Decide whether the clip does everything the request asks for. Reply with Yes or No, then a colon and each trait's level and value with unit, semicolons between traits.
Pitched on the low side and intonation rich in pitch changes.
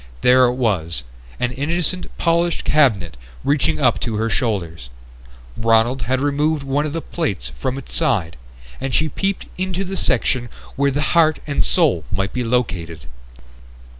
Yes: low, 130 Hz; wide, 6.9 semitones